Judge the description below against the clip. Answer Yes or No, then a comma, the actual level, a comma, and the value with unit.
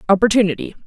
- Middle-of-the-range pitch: No, high, 205 Hz